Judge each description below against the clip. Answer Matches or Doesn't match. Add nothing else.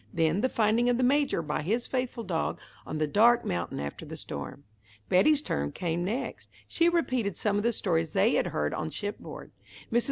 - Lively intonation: Matches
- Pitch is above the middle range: Matches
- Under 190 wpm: Doesn't match